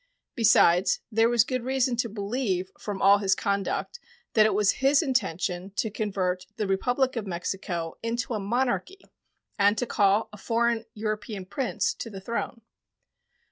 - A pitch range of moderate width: Yes, average, 3.5 semitones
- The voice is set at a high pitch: Yes, high, 215 Hz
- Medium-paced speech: Yes, average, 155 wpm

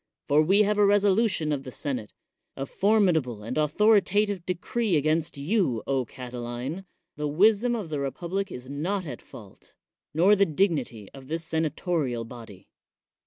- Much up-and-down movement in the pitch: Yes, wide, 6.9 semitones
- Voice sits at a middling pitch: Yes, medium, 160 Hz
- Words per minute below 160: Yes, average, 150 wpm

